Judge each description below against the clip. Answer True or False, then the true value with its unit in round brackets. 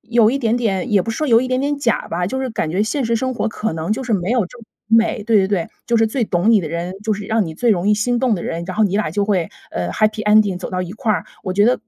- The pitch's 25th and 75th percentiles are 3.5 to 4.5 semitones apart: True (4.0 semitones)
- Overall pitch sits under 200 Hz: False (215 Hz)